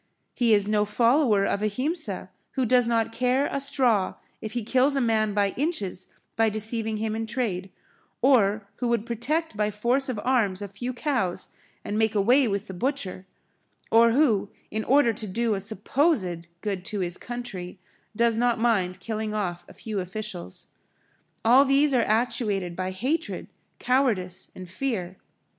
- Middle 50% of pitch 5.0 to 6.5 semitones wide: No, average, 3.9 semitones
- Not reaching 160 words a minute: No, average, 165 wpm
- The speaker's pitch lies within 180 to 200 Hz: No, high, 220 Hz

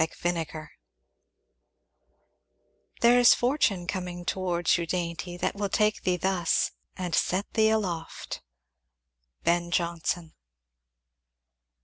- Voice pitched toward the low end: No, medium, 175 Hz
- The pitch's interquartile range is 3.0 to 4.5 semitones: No, narrow, 2.6 semitones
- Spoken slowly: Yes, slow, 105 wpm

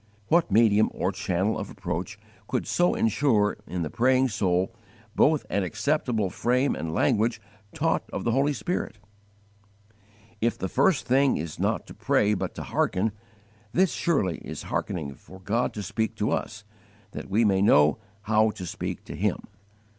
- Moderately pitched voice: No, low, 110 Hz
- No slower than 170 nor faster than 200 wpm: No, average, 160 wpm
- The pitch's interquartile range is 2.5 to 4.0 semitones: No, average, 4.7 semitones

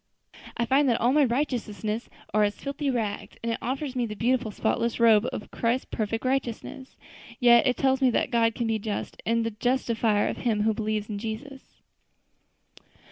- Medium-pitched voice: No, high, 235 Hz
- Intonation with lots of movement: No, average, 2.9 semitones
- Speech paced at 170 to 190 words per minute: Yes, average, 185 wpm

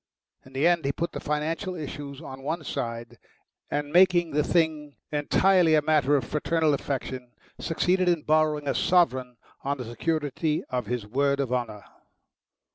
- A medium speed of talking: Yes, average, 160 wpm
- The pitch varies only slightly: No, average, 3.6 semitones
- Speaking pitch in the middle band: Yes, medium, 150 Hz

